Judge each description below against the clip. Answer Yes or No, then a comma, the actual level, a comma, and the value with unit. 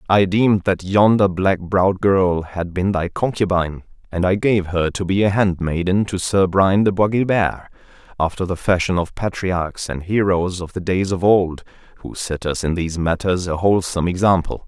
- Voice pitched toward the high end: No, very low, 95 Hz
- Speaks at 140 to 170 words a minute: No, average, 190 wpm